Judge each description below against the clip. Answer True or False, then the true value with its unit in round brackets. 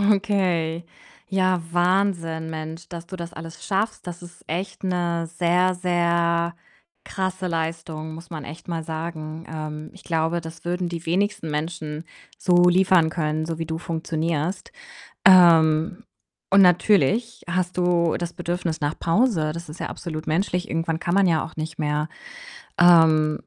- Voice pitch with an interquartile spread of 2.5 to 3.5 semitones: False (1.9 semitones)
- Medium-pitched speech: True (170 Hz)